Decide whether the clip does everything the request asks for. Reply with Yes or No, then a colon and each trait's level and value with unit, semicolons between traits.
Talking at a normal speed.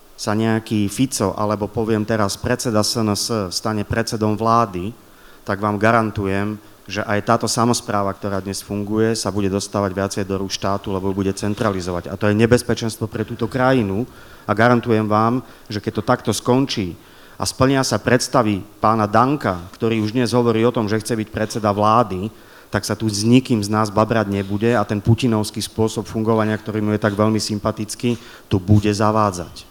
No: fast, 175 wpm